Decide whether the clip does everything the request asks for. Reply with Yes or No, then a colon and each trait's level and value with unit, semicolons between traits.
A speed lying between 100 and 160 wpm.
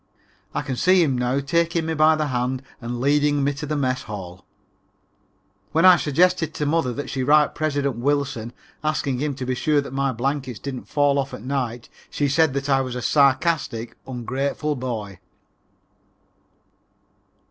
No: average, 175 wpm